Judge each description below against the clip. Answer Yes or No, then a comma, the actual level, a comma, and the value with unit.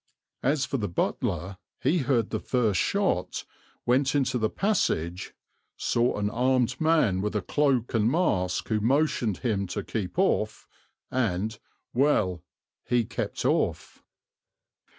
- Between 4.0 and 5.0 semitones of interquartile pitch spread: Yes, average, 4.7 semitones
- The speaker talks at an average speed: No, slow, 130 wpm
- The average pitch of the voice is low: Yes, low, 115 Hz